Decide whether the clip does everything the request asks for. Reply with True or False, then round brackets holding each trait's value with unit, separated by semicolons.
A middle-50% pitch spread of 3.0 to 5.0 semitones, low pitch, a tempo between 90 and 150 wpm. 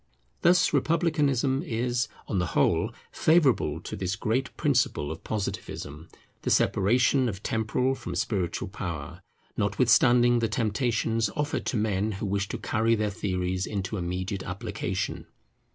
True (4.6 semitones; 110 Hz; 135 wpm)